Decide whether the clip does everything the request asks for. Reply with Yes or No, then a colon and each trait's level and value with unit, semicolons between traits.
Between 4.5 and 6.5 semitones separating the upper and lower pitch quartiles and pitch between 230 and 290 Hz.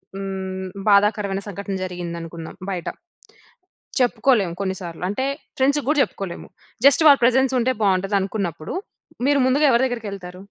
No: average, 4.8 semitones; high, 200 Hz